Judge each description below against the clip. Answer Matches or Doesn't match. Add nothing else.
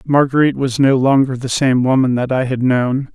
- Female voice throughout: Doesn't match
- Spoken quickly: Matches